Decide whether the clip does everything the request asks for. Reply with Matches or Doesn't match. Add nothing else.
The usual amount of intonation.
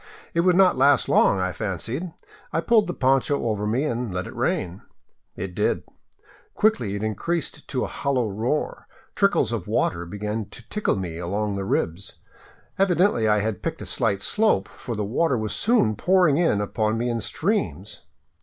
Doesn't match